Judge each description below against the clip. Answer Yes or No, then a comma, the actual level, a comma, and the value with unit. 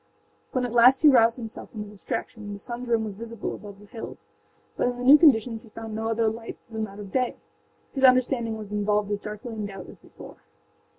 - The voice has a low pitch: No, high, 225 Hz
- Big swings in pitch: No, average, 2.7 semitones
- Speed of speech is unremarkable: No, fast, 225 wpm